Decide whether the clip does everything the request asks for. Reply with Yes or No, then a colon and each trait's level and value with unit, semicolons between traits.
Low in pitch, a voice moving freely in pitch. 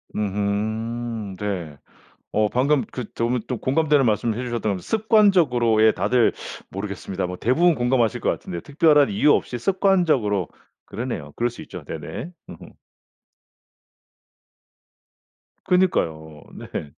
Yes: low, 115 Hz; wide, 5.9 semitones